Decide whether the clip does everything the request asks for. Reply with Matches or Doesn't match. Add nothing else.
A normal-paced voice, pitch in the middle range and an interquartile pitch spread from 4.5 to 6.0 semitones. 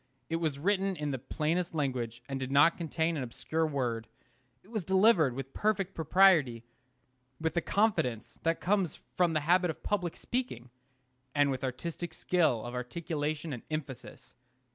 Matches